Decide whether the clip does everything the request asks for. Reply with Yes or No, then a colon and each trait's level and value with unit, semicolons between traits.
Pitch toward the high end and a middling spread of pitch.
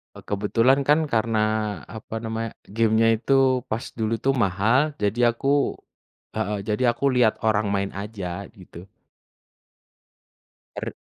No: low, 115 Hz; average, 3.3 semitones